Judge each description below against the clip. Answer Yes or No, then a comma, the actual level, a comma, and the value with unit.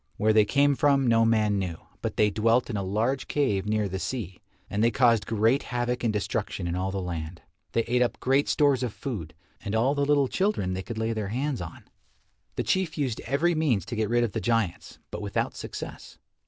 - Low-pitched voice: Yes, low, 115 Hz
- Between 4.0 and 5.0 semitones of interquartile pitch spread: Yes, average, 4.7 semitones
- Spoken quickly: Yes, fast, 220 wpm